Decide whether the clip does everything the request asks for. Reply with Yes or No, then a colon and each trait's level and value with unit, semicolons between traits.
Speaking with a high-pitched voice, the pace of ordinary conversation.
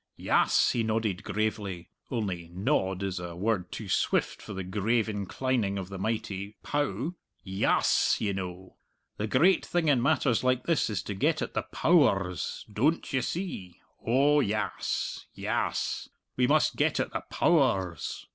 No: low, 110 Hz; average, 160 wpm